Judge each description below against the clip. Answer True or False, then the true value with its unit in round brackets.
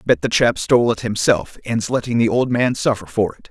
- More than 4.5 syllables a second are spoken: True (5.3 syllables/s)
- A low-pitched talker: True (110 Hz)